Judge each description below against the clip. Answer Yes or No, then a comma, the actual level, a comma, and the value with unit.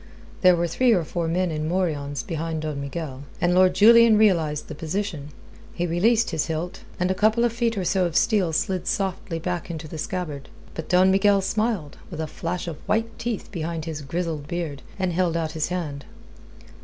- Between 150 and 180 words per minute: No, average, 195 wpm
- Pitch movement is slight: No, average, 3.4 semitones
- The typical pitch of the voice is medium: Yes, medium, 175 Hz